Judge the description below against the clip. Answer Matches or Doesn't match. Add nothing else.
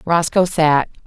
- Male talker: Doesn't match